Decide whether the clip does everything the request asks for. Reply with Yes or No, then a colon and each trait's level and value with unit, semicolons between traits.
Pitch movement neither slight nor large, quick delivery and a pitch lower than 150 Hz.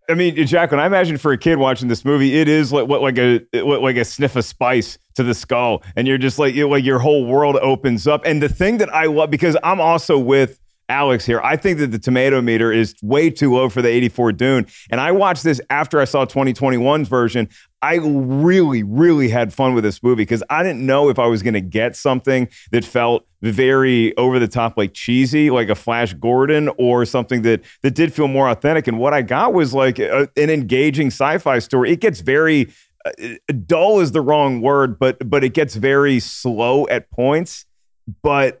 Yes: average, 3.6 semitones; fast, 215 wpm; low, 135 Hz